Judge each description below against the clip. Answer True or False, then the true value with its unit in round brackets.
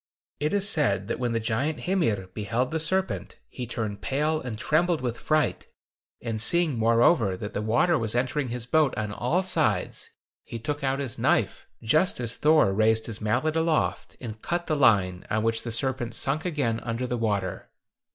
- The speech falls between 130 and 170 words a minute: False (185 wpm)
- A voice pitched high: False (120 Hz)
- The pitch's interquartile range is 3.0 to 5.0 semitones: False (5.6 semitones)